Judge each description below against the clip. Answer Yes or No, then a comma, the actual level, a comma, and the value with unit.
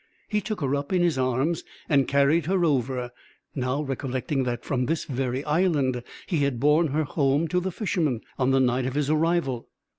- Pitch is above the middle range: No, medium, 140 Hz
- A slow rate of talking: No, average, 190 wpm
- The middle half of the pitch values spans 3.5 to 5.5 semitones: Yes, average, 4.0 semitones